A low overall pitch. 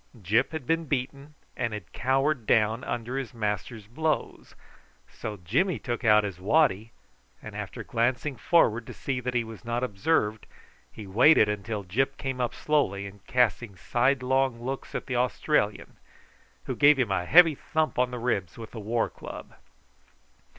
Yes: low, 120 Hz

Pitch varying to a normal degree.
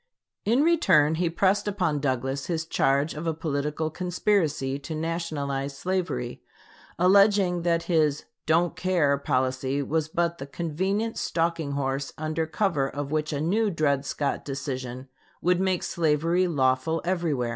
Yes: average, 3.9 semitones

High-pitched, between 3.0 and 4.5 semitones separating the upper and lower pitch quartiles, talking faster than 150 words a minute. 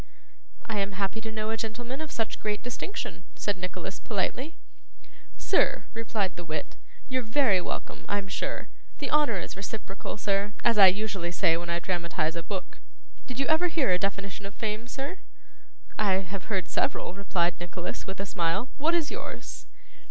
Yes: high, 205 Hz; average, 4.1 semitones; average, 175 wpm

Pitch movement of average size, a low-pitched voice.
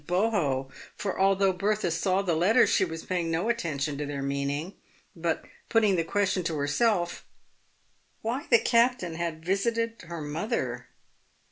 No: average, 4.8 semitones; medium, 175 Hz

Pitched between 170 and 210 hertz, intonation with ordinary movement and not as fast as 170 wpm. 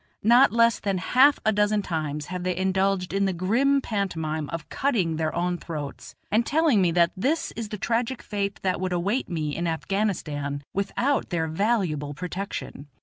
No: high, 190 Hz; average, 4.7 semitones; average, 175 wpm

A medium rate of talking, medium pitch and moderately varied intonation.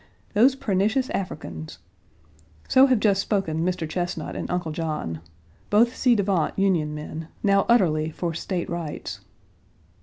No: slow, 130 wpm; medium, 180 Hz; average, 4.6 semitones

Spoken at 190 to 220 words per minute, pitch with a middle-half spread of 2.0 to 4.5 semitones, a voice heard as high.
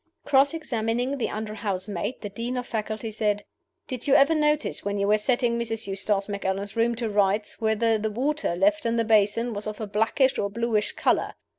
Yes: average, 195 wpm; average, 2.7 semitones; high, 220 Hz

